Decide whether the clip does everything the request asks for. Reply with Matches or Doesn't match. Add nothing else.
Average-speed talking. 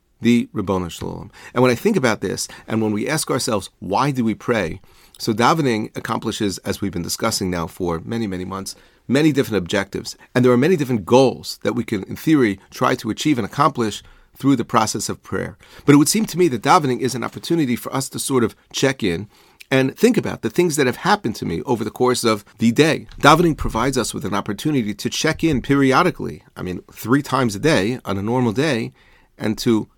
Doesn't match